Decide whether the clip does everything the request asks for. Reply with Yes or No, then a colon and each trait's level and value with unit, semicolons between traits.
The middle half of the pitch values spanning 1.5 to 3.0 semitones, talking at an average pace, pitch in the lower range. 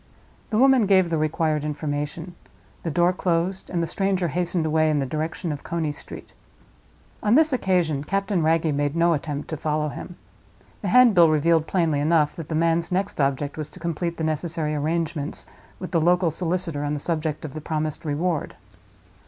No: average, 2.7 semitones; average, 180 wpm; medium, 165 Hz